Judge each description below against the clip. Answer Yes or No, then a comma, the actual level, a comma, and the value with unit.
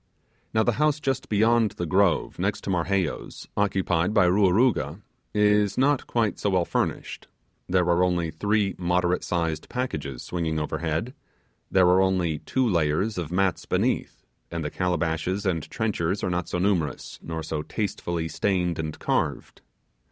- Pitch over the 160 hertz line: No, very low, 90 Hz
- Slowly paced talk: No, average, 155 wpm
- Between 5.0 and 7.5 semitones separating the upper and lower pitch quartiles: No, average, 3.7 semitones